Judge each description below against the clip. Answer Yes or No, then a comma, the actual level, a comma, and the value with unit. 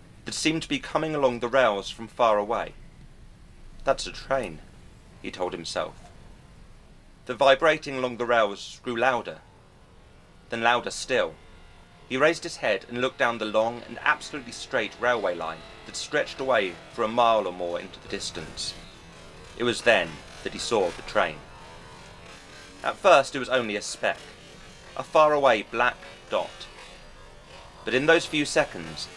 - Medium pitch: No, low, 125 Hz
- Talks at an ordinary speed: Yes, average, 155 wpm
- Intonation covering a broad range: Yes, wide, 5.8 semitones